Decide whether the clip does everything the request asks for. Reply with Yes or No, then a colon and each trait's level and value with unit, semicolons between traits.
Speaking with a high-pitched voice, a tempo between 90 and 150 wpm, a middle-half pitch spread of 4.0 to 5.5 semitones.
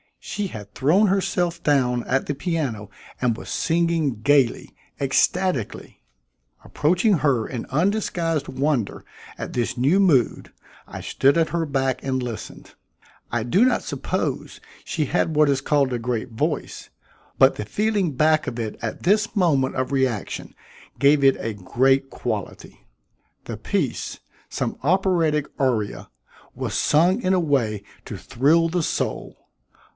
No: medium, 140 Hz; average, 140 wpm; average, 5.2 semitones